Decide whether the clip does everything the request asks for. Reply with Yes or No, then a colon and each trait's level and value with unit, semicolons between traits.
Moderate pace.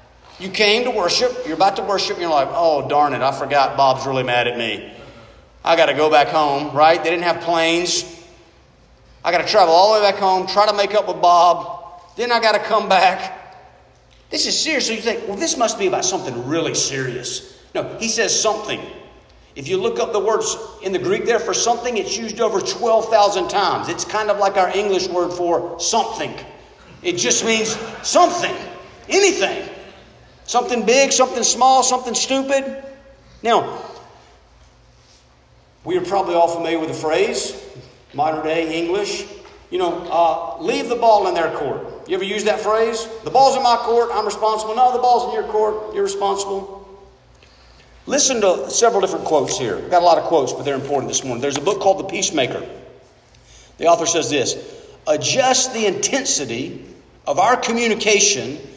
Yes: average, 180 wpm